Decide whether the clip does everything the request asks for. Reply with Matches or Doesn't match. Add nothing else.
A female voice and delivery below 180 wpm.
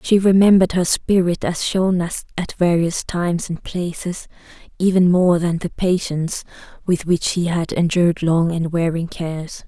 Matches